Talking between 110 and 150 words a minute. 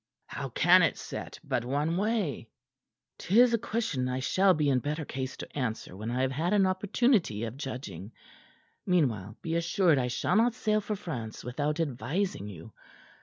No: average, 170 wpm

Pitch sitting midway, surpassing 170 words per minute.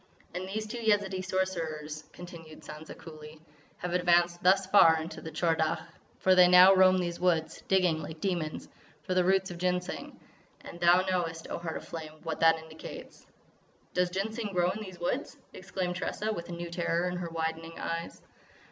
Yes: medium, 175 Hz; average, 180 wpm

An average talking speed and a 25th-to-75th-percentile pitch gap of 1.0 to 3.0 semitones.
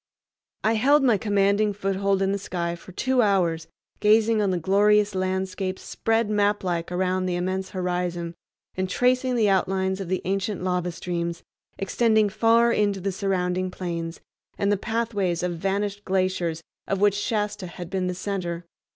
Yes: average, 160 wpm; narrow, 2.4 semitones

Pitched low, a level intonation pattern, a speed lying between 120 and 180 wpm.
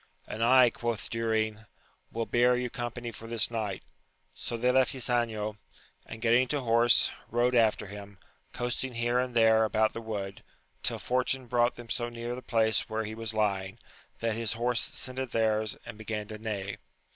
Yes: low, 115 Hz; narrow, 1.8 semitones; average, 175 wpm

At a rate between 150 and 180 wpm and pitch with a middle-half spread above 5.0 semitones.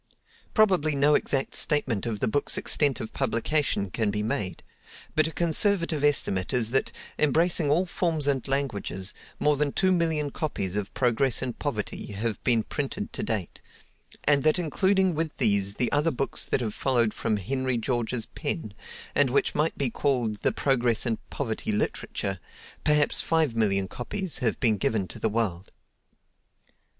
Yes: average, 160 wpm; wide, 5.4 semitones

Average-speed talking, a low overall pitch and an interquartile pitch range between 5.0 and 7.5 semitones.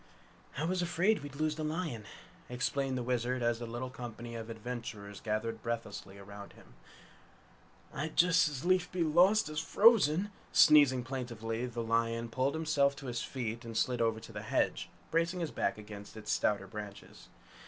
Yes: average, 170 wpm; low, 125 Hz; average, 5.3 semitones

